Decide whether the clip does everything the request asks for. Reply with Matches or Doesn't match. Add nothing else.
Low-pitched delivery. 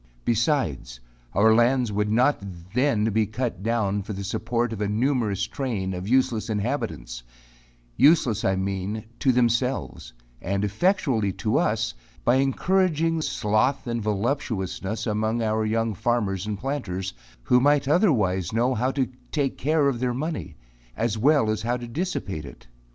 Matches